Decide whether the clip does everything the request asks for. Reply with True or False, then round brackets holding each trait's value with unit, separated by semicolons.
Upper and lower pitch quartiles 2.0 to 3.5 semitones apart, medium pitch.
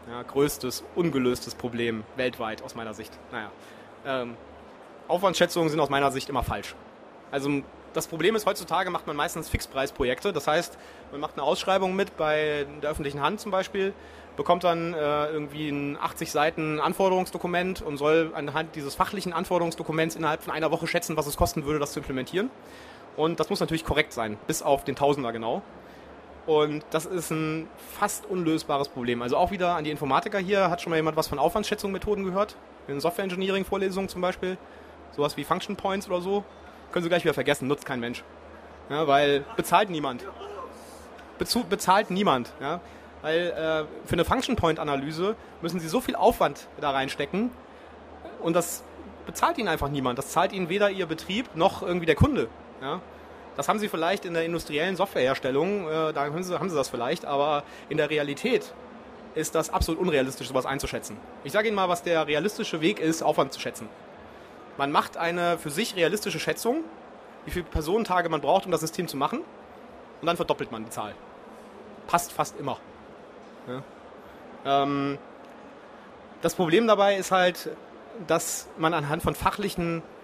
False (4.5 semitones; 160 Hz)